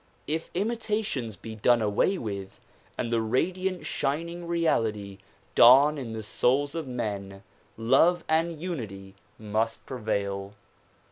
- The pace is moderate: No, slow, 120 wpm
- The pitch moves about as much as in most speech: No, wide, 7.7 semitones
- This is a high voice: No, low, 125 Hz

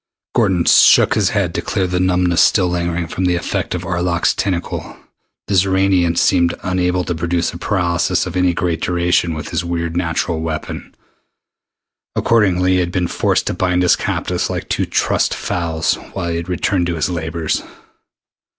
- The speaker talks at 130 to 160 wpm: No, average, 170 wpm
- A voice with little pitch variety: Yes, narrow, 1.2 semitones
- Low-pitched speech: Yes, very low, 90 Hz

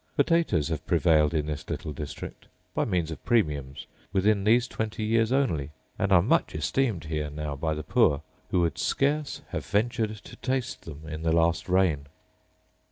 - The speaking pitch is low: Yes, very low, 85 Hz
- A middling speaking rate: Yes, average, 170 wpm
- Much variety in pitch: Yes, wide, 6.6 semitones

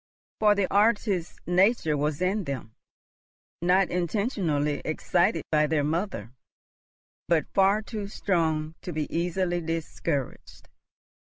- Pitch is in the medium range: Yes, medium, 175 Hz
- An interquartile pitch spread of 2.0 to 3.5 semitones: No, average, 4.2 semitones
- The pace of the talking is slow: Yes, slow, 110 wpm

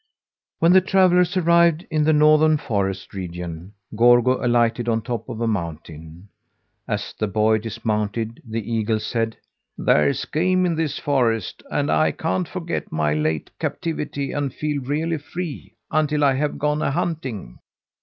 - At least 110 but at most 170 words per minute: Yes, average, 150 wpm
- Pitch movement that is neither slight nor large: No, wide, 6.9 semitones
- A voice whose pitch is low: Yes, low, 120 Hz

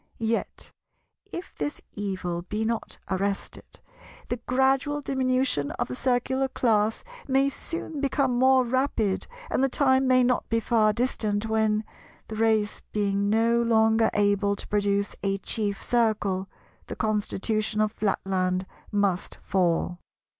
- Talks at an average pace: No, slow, 130 wpm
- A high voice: Yes, high, 220 Hz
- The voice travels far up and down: No, average, 3.9 semitones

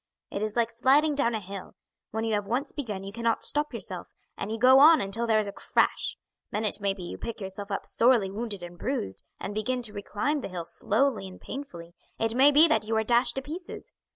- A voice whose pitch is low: No, high, 225 Hz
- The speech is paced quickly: Yes, fast, 235 wpm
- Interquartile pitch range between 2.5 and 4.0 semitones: No, average, 4.4 semitones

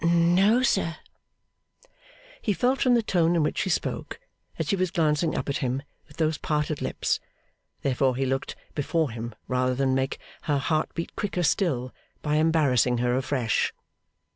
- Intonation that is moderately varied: Yes, average, 4.5 semitones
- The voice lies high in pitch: No, medium, 150 Hz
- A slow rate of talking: No, average, 165 wpm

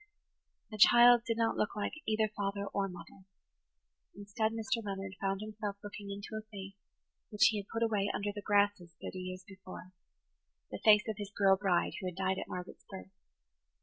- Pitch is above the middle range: Yes, high, 200 Hz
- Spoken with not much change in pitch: Yes, narrow, 1.9 semitones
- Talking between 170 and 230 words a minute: Yes, average, 180 wpm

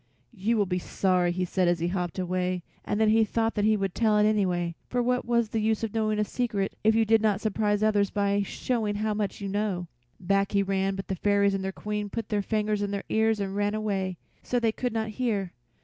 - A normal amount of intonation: No, narrow, 2.0 semitones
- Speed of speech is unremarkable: No, fast, 240 wpm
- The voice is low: No, high, 205 Hz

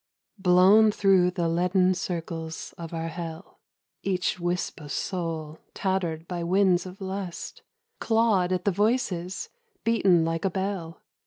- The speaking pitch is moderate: Yes, medium, 180 Hz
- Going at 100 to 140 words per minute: Yes, slow, 135 wpm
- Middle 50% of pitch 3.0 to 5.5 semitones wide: No, narrow, 2.4 semitones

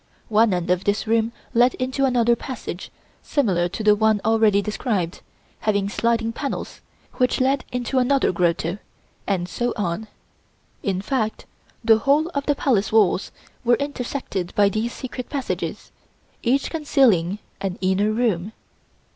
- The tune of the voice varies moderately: Yes, average, 4.4 semitones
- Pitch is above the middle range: Yes, high, 225 Hz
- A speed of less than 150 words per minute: Yes, average, 140 wpm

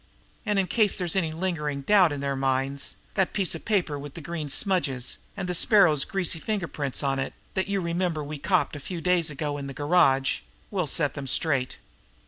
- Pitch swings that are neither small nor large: Yes, average, 4.7 semitones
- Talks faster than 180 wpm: Yes, fast, 205 wpm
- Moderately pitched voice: Yes, medium, 160 Hz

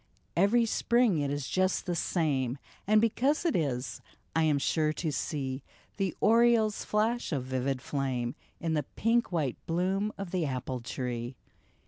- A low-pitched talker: No, medium, 160 Hz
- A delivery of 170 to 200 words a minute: No, average, 160 wpm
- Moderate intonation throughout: No, wide, 7.9 semitones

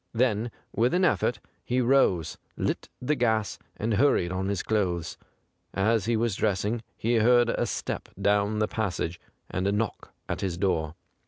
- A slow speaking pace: No, average, 165 wpm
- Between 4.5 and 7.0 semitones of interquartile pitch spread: No, average, 3.6 semitones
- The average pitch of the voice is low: Yes, low, 110 Hz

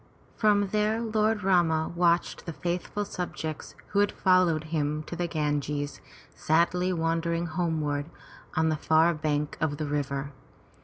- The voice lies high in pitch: No, medium, 165 Hz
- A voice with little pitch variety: No, average, 3.0 semitones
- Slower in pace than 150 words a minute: Yes, slow, 135 wpm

